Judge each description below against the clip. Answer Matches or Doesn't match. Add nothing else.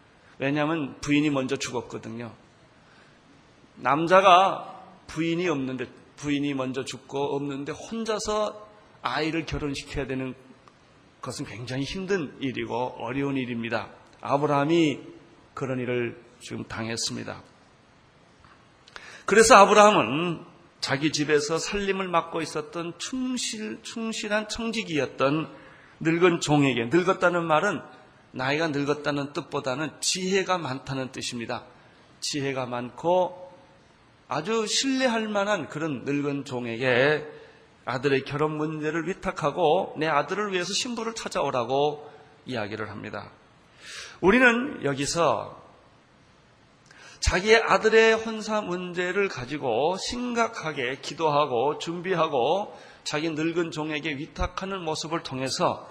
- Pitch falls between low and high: Matches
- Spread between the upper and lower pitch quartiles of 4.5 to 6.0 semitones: Matches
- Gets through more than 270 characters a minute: Doesn't match